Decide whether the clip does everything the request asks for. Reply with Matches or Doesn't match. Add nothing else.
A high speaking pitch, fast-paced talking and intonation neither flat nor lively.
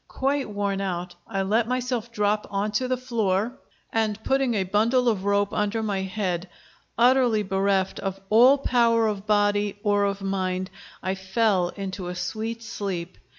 Doesn't match